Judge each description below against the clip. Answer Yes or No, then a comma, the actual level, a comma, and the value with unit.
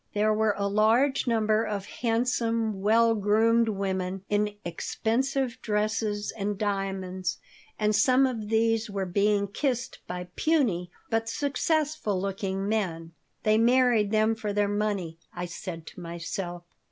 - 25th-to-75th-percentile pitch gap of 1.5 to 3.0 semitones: Yes, average, 2.7 semitones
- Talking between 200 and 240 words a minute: No, slow, 135 wpm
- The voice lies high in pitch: Yes, high, 210 Hz